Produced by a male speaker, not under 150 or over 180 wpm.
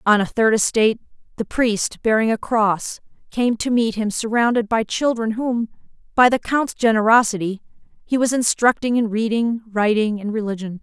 No: female; average, 160 wpm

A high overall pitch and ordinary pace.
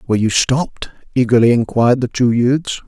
No: low, 120 Hz; average, 165 wpm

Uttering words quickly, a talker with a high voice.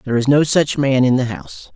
No: fast, 275 wpm; low, 135 Hz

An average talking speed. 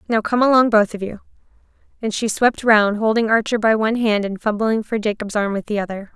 No: fast, 225 wpm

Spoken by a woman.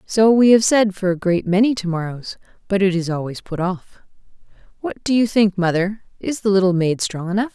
Yes: female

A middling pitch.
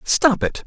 No: high, 195 Hz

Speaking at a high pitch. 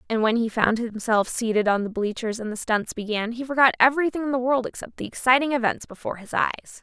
Yes: high, 235 Hz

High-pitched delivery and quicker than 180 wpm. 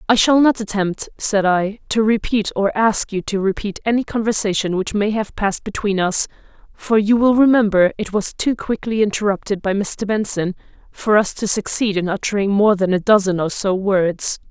Yes: high, 205 Hz; average, 190 wpm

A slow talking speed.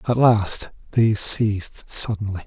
Yes: slow, 120 wpm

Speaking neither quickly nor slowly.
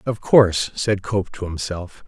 Yes: average, 175 wpm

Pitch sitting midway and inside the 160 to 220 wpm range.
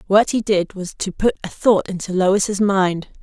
No: high, 195 Hz; fast, 205 wpm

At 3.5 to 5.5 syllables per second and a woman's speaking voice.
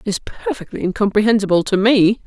No: 5.9 syllables/s; female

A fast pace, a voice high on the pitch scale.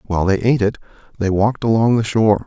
No: fast, 220 wpm; low, 105 Hz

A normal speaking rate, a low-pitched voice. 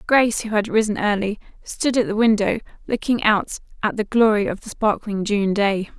No: average, 190 wpm; high, 210 Hz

